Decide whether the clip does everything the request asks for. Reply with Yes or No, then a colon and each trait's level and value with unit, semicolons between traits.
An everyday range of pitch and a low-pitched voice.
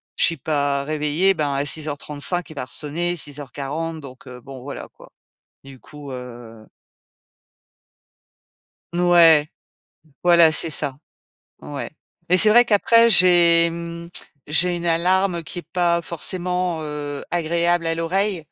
No: average, 3.3 semitones; medium, 165 Hz